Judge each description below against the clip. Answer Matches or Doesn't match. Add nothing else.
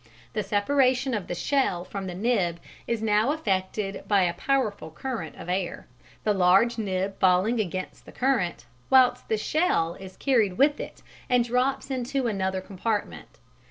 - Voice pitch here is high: Matches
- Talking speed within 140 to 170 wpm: Matches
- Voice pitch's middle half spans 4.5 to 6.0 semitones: Matches